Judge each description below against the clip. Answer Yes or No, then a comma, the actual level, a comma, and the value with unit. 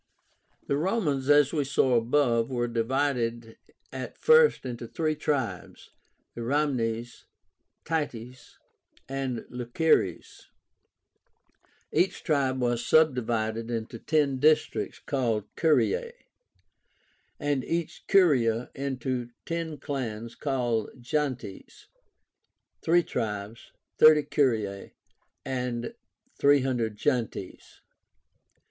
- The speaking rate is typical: No, slow, 85 wpm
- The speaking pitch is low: Yes, low, 130 Hz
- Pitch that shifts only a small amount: No, average, 4.1 semitones